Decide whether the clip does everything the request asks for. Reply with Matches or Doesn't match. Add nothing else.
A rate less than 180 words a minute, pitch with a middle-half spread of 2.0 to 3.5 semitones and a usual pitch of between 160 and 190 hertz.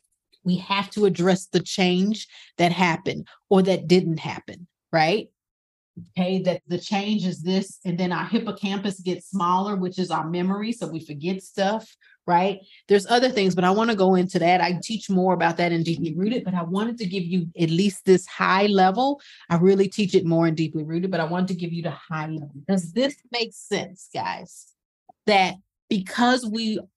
Doesn't match